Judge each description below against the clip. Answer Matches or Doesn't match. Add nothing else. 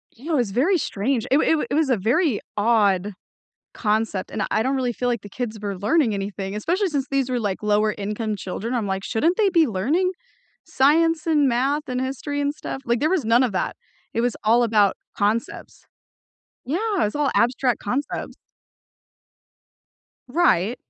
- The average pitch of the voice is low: Doesn't match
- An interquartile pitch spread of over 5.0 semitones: Matches